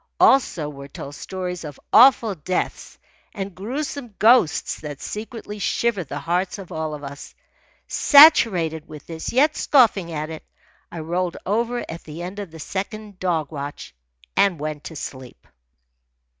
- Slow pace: No, average, 150 wpm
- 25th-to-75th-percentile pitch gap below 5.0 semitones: No, wide, 5.6 semitones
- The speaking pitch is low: No, medium, 180 Hz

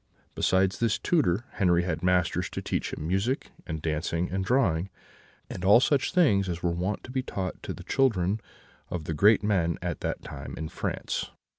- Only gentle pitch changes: No, average, 3.8 semitones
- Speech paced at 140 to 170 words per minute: No, average, 185 wpm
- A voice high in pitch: No, very low, 95 Hz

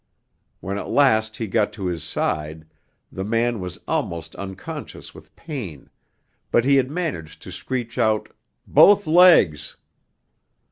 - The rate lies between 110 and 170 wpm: Yes, slow, 135 wpm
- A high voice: No, low, 110 Hz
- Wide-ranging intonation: Yes, wide, 6.9 semitones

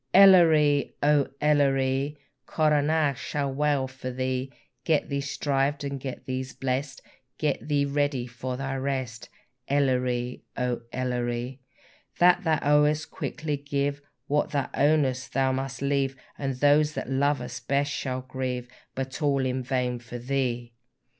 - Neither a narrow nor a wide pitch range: No, narrow, 2.1 semitones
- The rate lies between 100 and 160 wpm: Yes, slow, 135 wpm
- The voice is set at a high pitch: No, low, 135 Hz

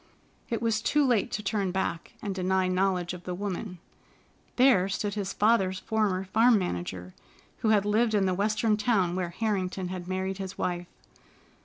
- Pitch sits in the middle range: No, high, 195 Hz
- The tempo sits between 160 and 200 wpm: Yes, average, 170 wpm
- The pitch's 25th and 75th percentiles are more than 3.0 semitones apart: No, average, 2.7 semitones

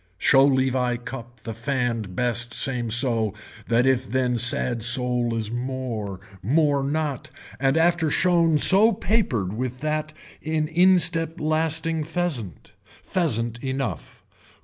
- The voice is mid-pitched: No, low, 130 Hz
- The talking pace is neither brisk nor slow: No, slow, 125 wpm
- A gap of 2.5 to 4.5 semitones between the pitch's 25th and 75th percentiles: No, average, 4.9 semitones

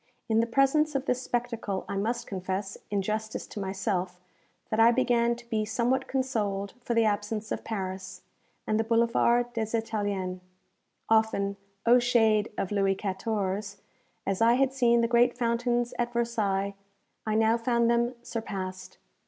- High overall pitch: Yes, high, 225 Hz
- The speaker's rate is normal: Yes, average, 155 wpm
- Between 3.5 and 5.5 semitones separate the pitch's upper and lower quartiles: No, average, 3.0 semitones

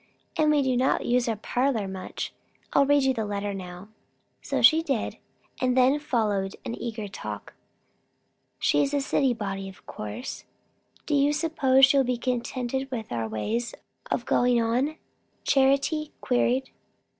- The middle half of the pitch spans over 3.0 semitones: Yes, average, 4.3 semitones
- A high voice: Yes, very high, 250 Hz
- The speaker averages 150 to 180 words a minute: Yes, average, 155 wpm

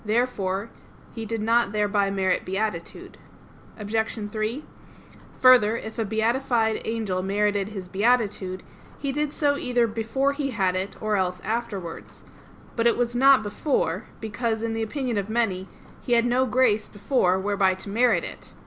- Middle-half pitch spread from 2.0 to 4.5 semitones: Yes, average, 3.1 semitones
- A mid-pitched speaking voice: No, high, 220 Hz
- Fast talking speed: No, average, 155 wpm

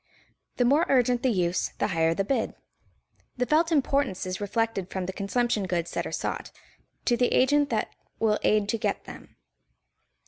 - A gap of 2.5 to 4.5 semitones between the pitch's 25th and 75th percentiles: No, wide, 5.4 semitones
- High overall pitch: Yes, high, 225 Hz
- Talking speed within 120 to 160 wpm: No, average, 175 wpm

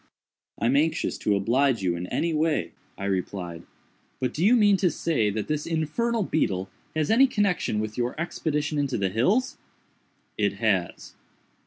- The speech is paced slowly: No, average, 165 wpm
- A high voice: No, medium, 145 Hz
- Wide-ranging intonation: Yes, wide, 8.3 semitones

